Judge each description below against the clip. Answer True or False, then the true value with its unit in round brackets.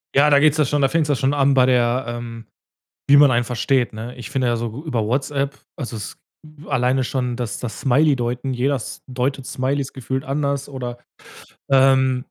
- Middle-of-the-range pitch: False (130 Hz)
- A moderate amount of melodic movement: False (2.3 semitones)